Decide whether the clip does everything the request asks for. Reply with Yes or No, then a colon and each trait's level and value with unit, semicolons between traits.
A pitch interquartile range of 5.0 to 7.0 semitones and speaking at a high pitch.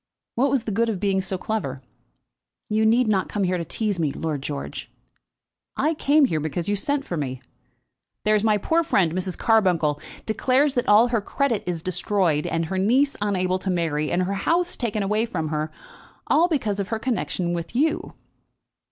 Yes: average, 5.3 semitones; high, 200 Hz